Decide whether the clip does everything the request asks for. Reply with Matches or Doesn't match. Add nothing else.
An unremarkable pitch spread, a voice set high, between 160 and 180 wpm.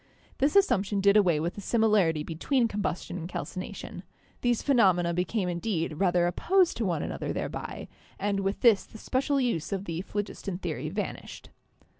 Matches